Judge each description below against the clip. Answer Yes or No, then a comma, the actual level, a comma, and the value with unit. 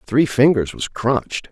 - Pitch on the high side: No, low, 130 Hz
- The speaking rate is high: No, average, 160 wpm